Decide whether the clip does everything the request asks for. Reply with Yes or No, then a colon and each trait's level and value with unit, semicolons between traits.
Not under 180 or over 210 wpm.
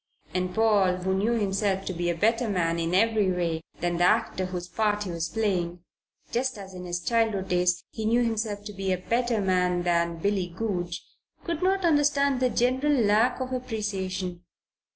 Yes: average, 185 wpm